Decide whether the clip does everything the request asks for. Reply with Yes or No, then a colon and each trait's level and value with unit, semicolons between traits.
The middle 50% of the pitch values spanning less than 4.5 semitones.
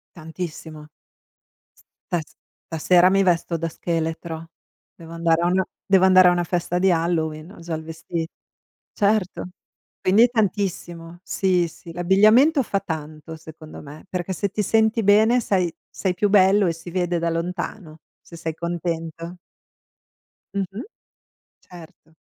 Yes: average, 2.7 semitones